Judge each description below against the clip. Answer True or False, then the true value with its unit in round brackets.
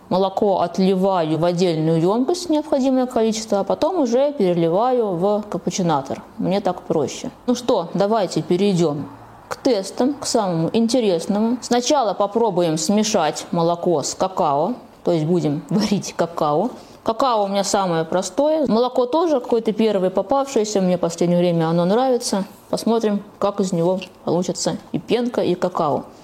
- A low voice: False (200 Hz)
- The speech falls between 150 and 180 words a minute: False (140 wpm)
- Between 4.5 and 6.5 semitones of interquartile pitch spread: True (5.0 semitones)